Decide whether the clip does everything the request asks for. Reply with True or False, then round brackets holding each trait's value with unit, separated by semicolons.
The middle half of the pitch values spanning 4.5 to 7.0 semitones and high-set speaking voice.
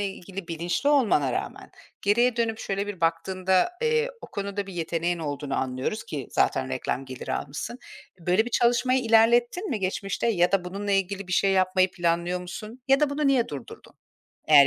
True (5.1 semitones; 195 Hz)